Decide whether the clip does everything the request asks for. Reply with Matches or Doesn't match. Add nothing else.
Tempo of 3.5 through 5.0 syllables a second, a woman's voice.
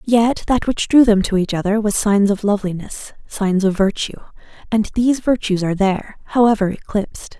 Doesn't match